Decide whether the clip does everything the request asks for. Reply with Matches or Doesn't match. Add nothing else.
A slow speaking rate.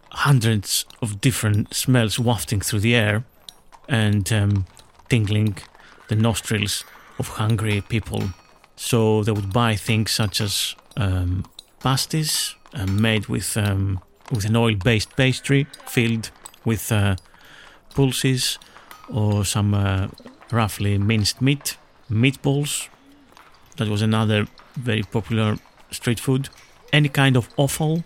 Matches